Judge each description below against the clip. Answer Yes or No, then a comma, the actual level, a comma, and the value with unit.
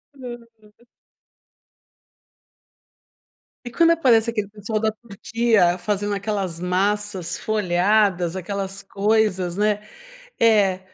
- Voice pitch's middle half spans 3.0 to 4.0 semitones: No, narrow, 2.5 semitones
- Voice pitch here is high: Yes, high, 205 Hz